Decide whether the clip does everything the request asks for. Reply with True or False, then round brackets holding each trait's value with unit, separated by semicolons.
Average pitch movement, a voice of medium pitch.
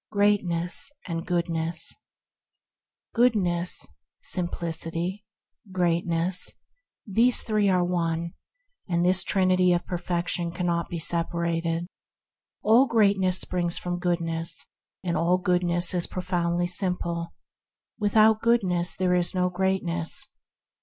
False (1.6 semitones; 175 Hz)